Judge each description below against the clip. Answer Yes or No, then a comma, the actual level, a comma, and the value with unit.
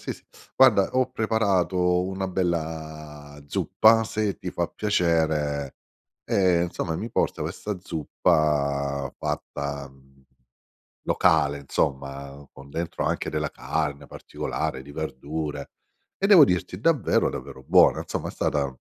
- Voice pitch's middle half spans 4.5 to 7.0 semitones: Yes, average, 4.9 semitones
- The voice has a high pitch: No, very low, 80 Hz